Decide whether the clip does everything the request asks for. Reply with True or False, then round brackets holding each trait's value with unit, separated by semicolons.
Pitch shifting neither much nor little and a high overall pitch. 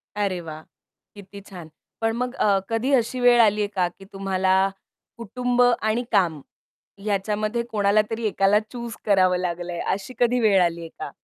True (3.6 semitones; 205 Hz)